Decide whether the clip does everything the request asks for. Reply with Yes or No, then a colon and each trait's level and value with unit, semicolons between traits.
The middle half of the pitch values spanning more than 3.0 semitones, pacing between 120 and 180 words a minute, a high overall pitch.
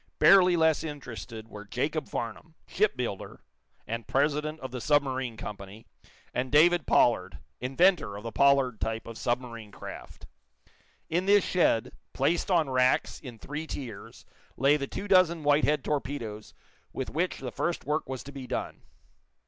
No: average, 5.1 semitones; average, 150 wpm; low, 135 Hz